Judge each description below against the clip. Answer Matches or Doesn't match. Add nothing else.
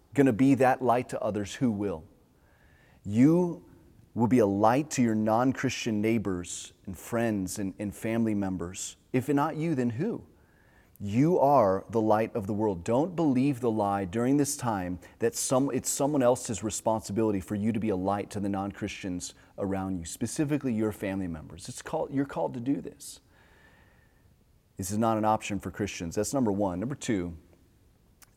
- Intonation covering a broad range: Doesn't match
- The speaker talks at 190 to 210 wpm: Doesn't match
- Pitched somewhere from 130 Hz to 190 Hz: Doesn't match